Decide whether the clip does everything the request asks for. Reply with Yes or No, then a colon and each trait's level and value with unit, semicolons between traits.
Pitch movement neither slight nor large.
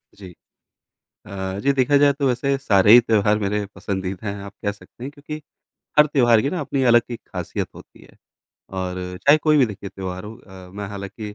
No: wide, 5.7 semitones